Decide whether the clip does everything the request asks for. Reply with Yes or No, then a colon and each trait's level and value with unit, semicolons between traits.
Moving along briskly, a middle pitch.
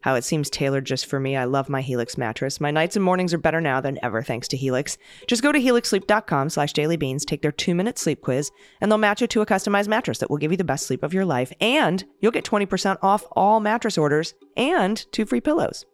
Yes: fast, 250 wpm; medium, 165 Hz